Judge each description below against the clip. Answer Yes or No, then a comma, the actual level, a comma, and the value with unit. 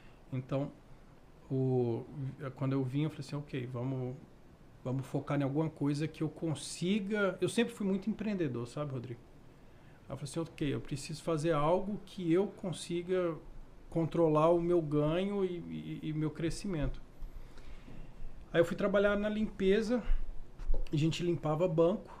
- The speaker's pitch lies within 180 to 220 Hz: No, medium, 155 Hz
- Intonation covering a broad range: No, average, 4.8 semitones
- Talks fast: No, average, 145 wpm